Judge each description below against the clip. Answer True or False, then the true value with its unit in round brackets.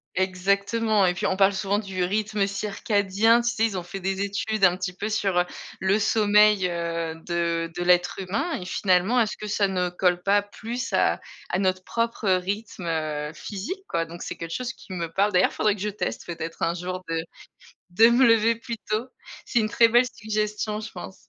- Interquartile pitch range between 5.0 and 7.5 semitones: False (3.1 semitones)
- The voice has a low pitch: False (195 Hz)